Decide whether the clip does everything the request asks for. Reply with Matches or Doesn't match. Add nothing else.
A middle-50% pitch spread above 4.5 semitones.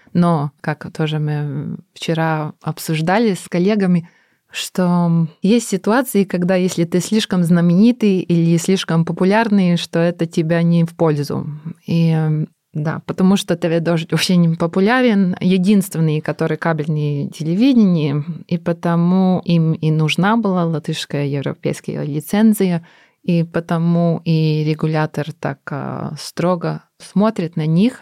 Doesn't match